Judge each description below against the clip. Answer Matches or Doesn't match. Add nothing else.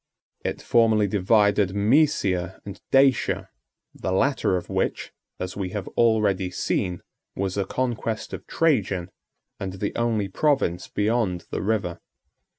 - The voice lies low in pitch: Matches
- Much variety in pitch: Doesn't match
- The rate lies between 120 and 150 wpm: Matches